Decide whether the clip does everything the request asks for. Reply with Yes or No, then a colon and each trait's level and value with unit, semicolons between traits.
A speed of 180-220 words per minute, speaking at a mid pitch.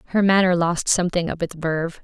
Yes: fast, 205 wpm; medium, 175 Hz